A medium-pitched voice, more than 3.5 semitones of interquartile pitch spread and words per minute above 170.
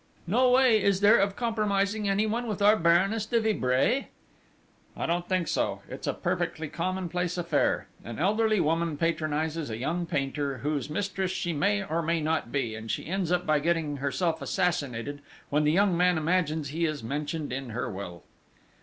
Yes: medium, 170 Hz; average, 5.0 semitones; average, 180 wpm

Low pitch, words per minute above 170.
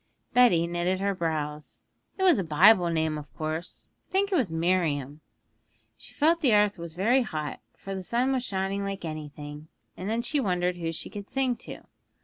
No: medium, 185 Hz; average, 190 wpm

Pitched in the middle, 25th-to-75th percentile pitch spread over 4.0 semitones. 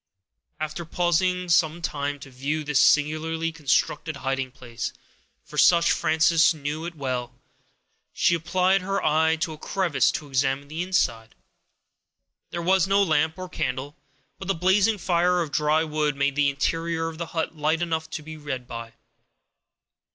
No: medium, 160 Hz; average, 3.0 semitones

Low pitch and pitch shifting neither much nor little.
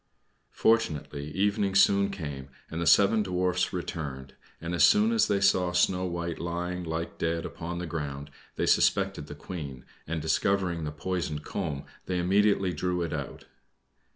Yes: very low, 85 Hz; average, 3.5 semitones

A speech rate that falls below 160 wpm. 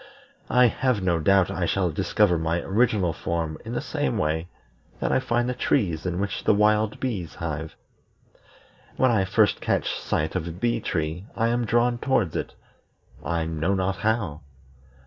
No: average, 170 wpm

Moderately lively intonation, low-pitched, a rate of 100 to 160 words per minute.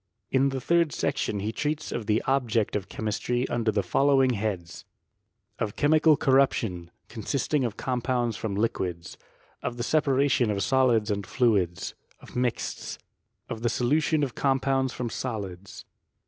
Yes: average, 4.1 semitones; low, 120 Hz; average, 145 wpm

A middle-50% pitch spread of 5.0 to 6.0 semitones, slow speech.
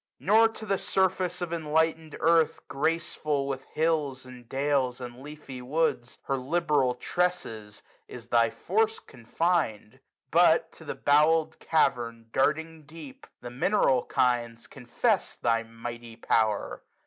Yes: average, 5.3 semitones; slow, 130 wpm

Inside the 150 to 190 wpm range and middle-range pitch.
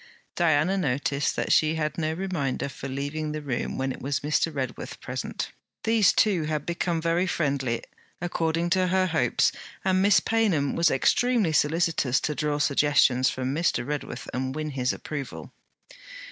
Yes: average, 160 wpm; medium, 155 Hz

